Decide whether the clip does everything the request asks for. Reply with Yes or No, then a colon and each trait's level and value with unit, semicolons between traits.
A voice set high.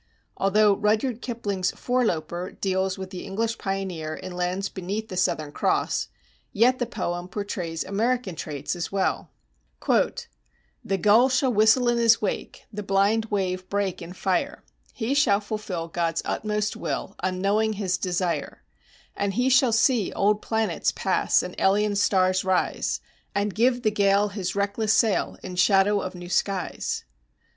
Yes: high, 200 Hz